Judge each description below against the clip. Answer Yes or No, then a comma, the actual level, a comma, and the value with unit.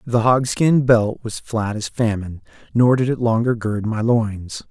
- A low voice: Yes, low, 115 Hz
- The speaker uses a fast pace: No, average, 180 wpm